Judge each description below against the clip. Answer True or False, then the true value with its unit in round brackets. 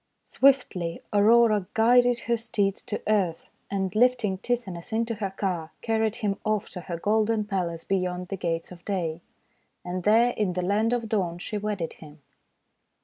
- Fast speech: False (160 wpm)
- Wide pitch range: False (3.8 semitones)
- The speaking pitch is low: False (205 Hz)